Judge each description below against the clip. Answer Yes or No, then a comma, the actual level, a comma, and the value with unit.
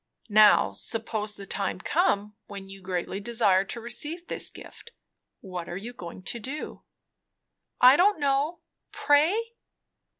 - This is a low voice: No, high, 225 Hz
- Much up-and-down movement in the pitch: Yes, wide, 6.7 semitones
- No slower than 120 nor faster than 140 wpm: Yes, slow, 135 wpm